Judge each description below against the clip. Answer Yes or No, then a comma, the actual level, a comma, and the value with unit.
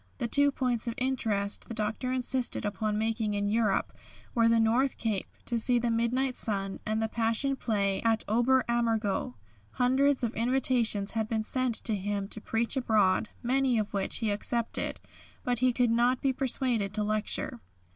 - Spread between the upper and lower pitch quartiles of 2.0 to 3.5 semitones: Yes, average, 2.8 semitones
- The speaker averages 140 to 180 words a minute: Yes, average, 175 wpm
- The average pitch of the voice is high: Yes, high, 230 Hz